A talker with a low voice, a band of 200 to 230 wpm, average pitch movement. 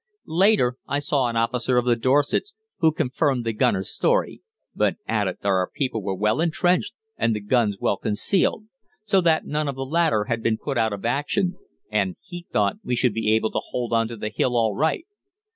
No: low, 125 Hz; fast, 205 wpm; wide, 6.2 semitones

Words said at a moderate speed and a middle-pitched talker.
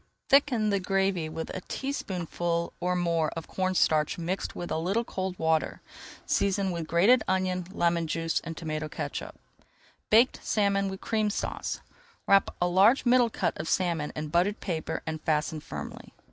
Yes: average, 160 wpm; medium, 180 Hz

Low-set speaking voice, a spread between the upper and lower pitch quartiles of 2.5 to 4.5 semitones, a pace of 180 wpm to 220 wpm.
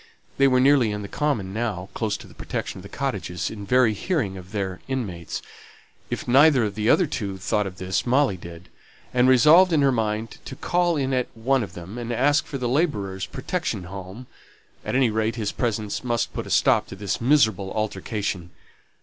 No: low, 110 Hz; average, 5.2 semitones; average, 200 wpm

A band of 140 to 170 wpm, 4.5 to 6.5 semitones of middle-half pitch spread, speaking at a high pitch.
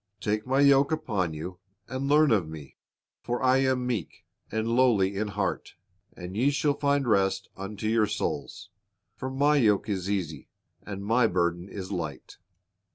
No: average, 160 wpm; average, 5.3 semitones; low, 110 Hz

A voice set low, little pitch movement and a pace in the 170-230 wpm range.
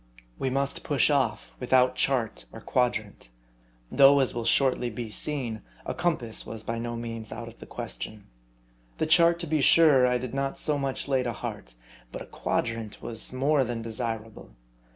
No: low, 125 Hz; average, 3.3 semitones; average, 175 wpm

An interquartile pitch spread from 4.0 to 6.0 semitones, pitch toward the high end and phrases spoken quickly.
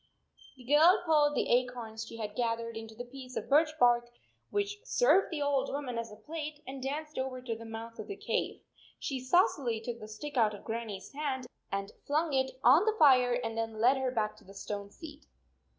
Yes: average, 4.6 semitones; very high, 255 Hz; fast, 215 wpm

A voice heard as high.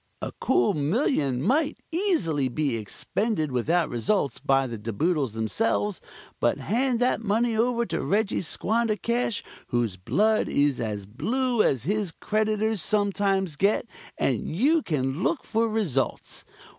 Yes: high, 200 Hz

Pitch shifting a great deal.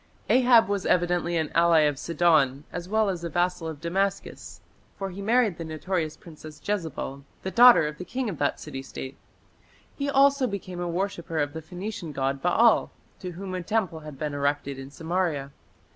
No: average, 4.5 semitones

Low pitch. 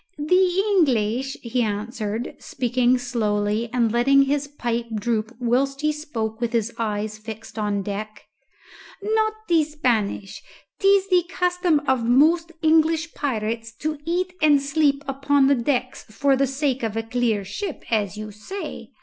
No: very high, 255 Hz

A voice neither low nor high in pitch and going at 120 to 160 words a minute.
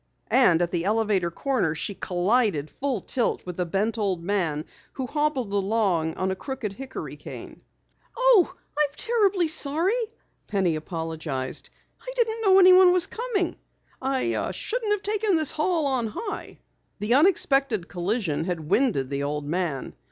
No: high, 225 Hz; average, 150 wpm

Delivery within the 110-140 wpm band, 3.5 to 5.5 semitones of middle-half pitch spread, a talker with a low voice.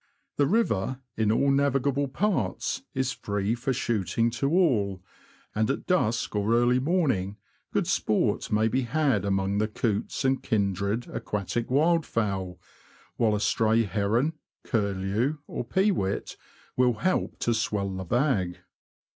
Yes: slow, 135 wpm; average, 5.1 semitones; low, 115 Hz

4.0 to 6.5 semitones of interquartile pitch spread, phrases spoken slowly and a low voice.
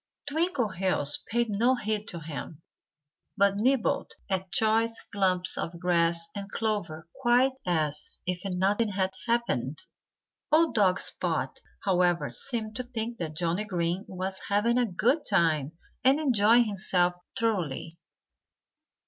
No: average, 4.8 semitones; slow, 125 wpm; high, 195 Hz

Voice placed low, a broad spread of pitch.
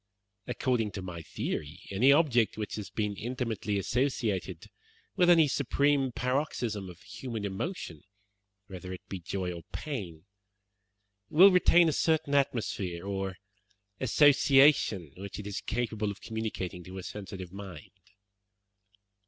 Yes: low, 105 Hz; wide, 6.0 semitones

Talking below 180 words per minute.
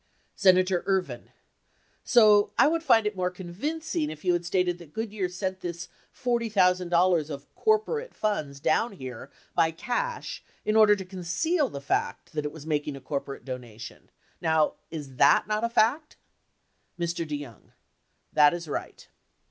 Yes: average, 150 wpm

